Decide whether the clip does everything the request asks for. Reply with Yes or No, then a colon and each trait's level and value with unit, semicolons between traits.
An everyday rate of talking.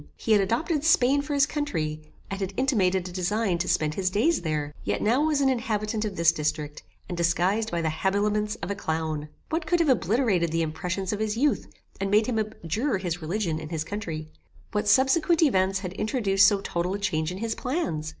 No: fast, 210 wpm